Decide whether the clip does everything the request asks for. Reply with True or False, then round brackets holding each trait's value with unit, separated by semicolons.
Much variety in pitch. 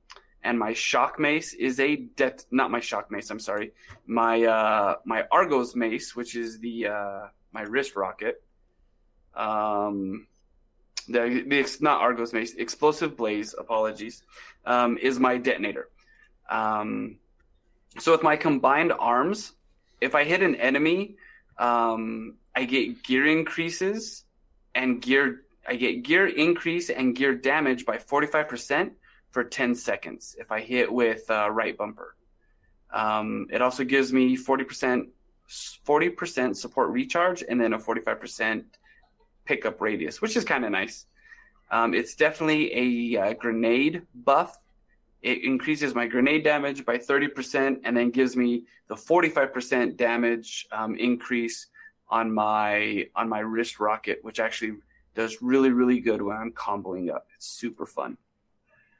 False (3.9 semitones)